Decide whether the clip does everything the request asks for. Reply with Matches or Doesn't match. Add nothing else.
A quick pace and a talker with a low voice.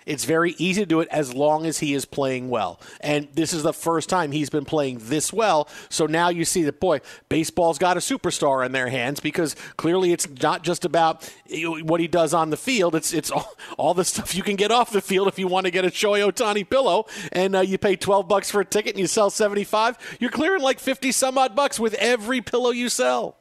Doesn't match